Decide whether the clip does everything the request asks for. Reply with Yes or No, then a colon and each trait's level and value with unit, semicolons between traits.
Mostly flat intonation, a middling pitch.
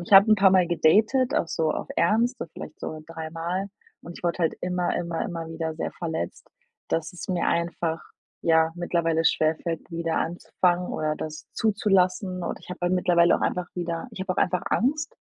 Yes: narrow, 2.0 semitones; medium, 175 Hz